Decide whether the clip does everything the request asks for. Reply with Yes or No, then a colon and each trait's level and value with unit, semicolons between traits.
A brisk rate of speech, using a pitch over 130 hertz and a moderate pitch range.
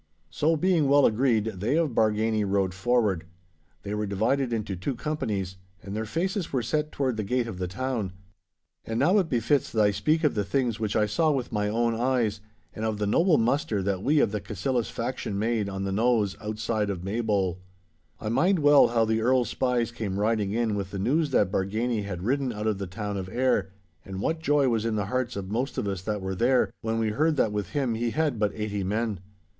No: fast, 220 wpm; low, 110 Hz; average, 4.1 semitones